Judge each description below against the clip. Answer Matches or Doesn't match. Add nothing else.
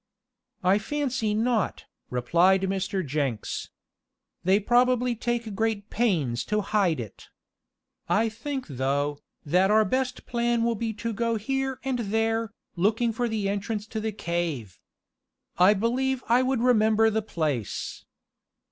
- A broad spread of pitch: Doesn't match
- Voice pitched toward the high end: Matches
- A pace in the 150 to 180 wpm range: Doesn't match